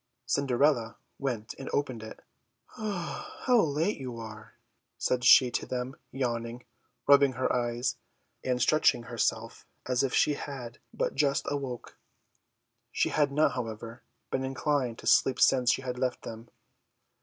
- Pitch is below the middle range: Yes, low, 125 Hz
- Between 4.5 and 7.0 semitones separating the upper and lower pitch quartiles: No, average, 2.9 semitones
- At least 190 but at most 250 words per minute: No, average, 140 wpm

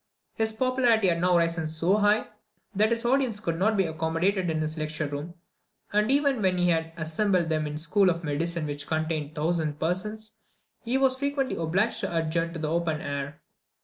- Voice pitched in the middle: Yes, medium, 170 Hz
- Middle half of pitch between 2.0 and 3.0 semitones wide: No, average, 5.1 semitones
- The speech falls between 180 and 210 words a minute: Yes, average, 190 wpm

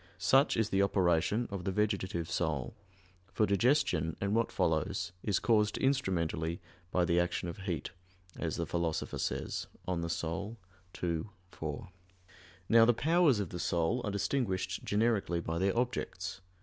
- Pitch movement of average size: Yes, average, 4.5 semitones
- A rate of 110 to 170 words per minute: Yes, average, 150 wpm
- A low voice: Yes, very low, 95 Hz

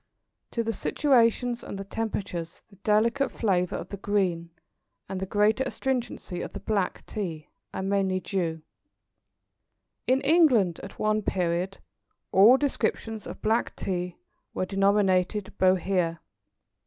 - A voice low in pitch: No, high, 200 Hz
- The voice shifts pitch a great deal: No, average, 3.5 semitones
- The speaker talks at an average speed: No, slow, 130 wpm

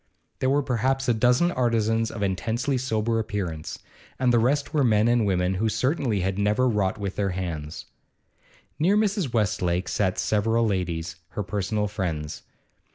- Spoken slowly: No, average, 160 wpm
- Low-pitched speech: Yes, low, 110 Hz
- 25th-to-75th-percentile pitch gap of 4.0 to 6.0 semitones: Yes, average, 4.7 semitones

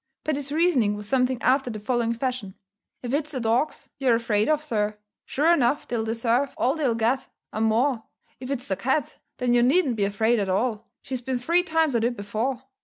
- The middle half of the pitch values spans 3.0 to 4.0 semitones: Yes, average, 3.4 semitones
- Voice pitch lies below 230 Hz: No, high, 245 Hz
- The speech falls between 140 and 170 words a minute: No, average, 200 wpm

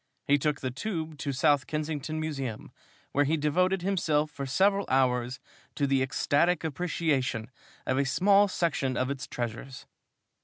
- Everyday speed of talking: Yes, average, 150 wpm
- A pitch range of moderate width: Yes, average, 3.5 semitones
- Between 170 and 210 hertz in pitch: No, medium, 145 Hz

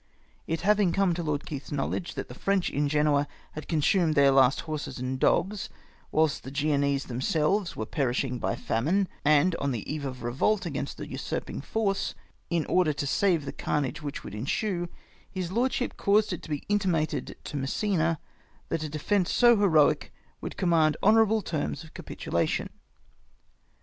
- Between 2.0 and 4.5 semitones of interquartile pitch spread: No, average, 5.1 semitones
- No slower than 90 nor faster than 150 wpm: No, average, 170 wpm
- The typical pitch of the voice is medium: Yes, medium, 155 Hz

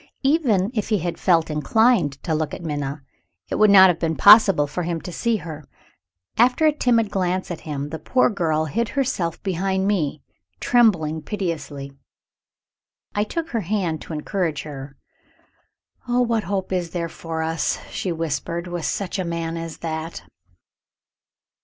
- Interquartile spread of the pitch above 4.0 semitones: Yes, average, 4.6 semitones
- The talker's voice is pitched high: No, medium, 175 Hz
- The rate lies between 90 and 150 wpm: No, average, 160 wpm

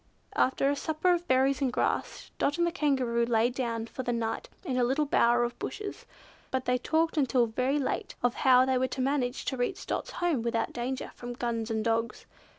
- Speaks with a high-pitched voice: Yes, very high, 255 Hz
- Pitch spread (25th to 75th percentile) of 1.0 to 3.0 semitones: Yes, average, 2.7 semitones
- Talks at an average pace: No, fast, 210 wpm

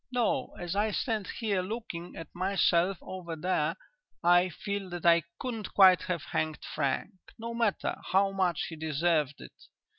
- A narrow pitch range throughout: No, average, 3.1 semitones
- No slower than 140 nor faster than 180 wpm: Yes, average, 155 wpm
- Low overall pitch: No, medium, 185 Hz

